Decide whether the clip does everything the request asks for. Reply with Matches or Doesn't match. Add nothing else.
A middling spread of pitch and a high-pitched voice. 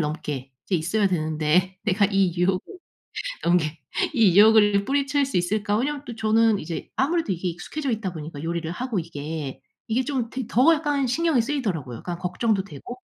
Doesn't match